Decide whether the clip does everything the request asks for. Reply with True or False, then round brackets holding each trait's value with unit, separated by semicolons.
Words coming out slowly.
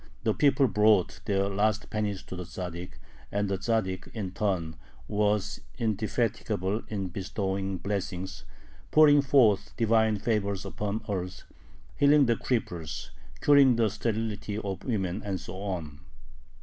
True (130 wpm)